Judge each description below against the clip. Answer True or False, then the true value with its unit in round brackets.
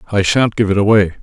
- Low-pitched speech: True (105 Hz)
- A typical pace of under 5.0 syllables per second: False (6.7 syllables/s)